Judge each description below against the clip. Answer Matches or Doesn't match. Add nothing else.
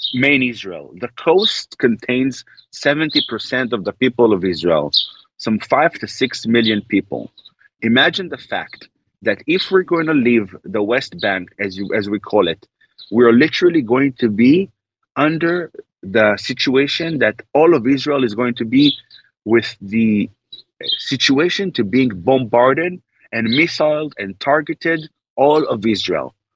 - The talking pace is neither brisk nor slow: Matches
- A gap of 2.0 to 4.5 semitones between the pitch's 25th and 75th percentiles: Doesn't match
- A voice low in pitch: Matches